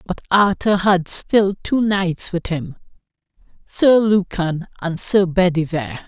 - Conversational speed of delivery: No, slow, 130 wpm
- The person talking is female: Yes, female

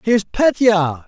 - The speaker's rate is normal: Yes, average, 165 wpm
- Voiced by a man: Yes, male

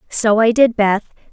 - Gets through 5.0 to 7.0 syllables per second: No, 4.0 syllables/s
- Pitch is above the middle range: Yes, high, 220 Hz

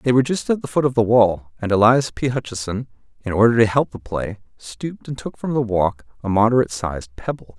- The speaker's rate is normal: No, fast, 230 wpm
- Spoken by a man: Yes, male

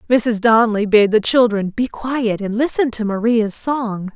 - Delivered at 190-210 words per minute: No, average, 175 wpm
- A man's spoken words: No, female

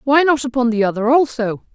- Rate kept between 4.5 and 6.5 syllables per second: Yes, 5.8 syllables/s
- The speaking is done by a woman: Yes, female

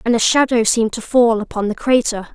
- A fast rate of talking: Yes, fast, 230 wpm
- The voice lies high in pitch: Yes, high, 230 Hz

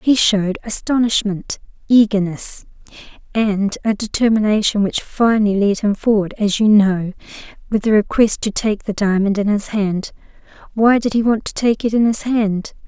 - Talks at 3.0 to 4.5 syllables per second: No, 4.8 syllables/s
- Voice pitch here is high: Yes, high, 210 Hz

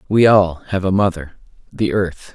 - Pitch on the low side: Yes, very low, 95 Hz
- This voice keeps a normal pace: Yes, average, 155 wpm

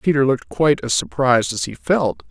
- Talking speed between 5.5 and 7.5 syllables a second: Yes, 6.0 syllables/s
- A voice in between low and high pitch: No, low, 125 Hz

